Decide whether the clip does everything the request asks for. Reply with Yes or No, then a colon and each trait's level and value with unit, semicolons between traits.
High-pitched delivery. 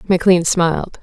No: medium, 180 Hz